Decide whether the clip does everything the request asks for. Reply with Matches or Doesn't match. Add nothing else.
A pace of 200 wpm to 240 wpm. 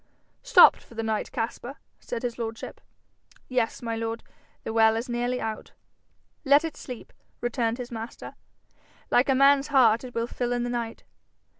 Doesn't match